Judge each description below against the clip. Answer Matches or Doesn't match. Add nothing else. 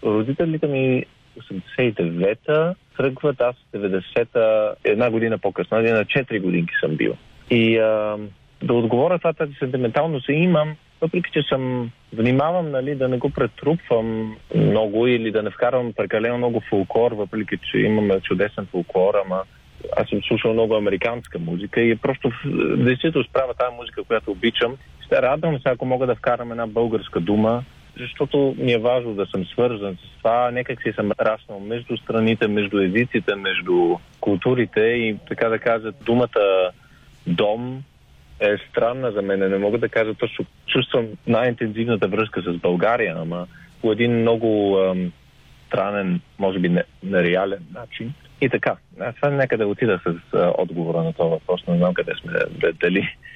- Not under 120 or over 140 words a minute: Doesn't match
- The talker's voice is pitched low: Matches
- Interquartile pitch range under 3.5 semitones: Doesn't match